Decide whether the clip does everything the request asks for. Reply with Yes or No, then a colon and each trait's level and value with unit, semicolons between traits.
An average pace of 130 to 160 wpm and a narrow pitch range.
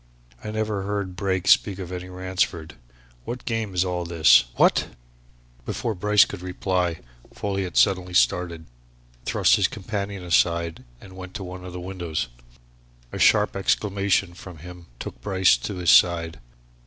Yes: average, 155 wpm; narrow, 2.2 semitones